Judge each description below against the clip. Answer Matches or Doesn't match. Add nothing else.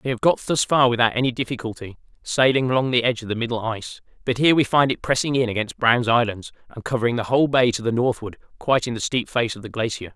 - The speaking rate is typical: Doesn't match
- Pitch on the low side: Matches